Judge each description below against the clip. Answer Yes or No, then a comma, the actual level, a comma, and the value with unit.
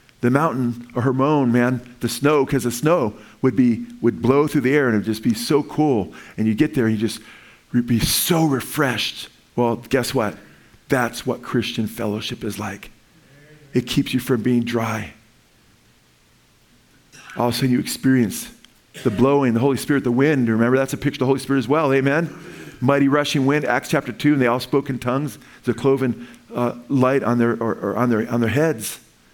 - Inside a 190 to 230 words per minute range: Yes, average, 200 wpm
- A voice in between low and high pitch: No, low, 125 Hz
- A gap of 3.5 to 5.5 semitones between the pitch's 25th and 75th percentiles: No, average, 3.0 semitones